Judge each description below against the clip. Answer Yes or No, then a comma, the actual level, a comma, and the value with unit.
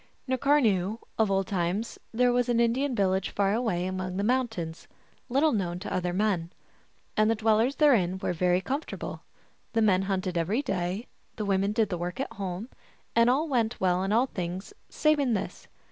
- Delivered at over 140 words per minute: Yes, average, 185 wpm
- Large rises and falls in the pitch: No, average, 4.6 semitones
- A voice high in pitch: Yes, high, 205 Hz